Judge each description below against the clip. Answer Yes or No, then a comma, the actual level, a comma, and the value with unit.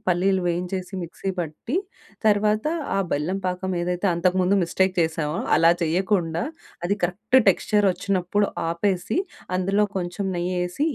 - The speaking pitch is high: No, medium, 180 Hz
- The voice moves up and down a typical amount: No, narrow, 2.3 semitones